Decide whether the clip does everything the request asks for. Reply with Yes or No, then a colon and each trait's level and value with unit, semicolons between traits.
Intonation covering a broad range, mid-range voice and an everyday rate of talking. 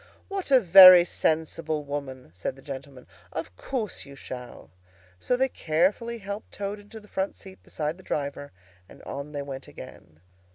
Yes: wide, 6.3 semitones; medium, 160 Hz; average, 165 wpm